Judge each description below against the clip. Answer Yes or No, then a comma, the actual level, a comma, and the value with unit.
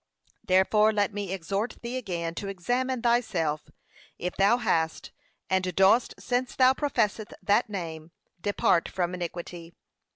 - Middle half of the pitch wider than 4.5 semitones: Yes, average, 5.1 semitones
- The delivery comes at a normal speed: No, slow, 130 wpm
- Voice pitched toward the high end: Yes, high, 195 Hz